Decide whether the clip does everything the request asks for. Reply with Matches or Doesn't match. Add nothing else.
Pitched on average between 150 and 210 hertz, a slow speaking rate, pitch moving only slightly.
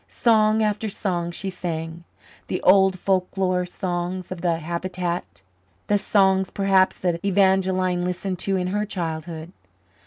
Matches